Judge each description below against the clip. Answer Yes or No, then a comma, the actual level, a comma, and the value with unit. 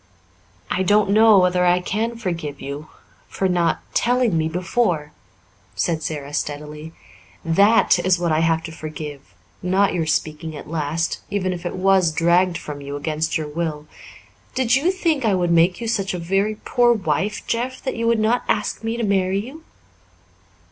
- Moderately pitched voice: Yes, medium, 180 Hz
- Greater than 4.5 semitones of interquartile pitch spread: Yes, average, 5.1 semitones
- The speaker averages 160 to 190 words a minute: Yes, average, 175 wpm